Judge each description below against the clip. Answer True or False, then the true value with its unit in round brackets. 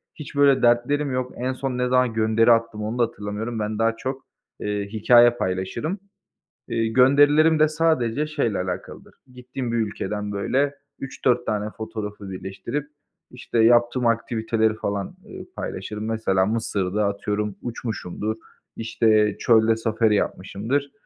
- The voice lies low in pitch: True (115 Hz)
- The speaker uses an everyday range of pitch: True (3.2 semitones)